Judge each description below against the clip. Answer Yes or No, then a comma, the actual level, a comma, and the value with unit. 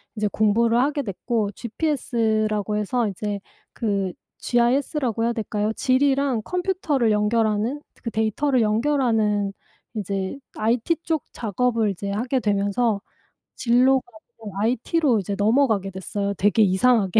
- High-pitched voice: Yes, high, 225 Hz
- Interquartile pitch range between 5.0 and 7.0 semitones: No, average, 3.5 semitones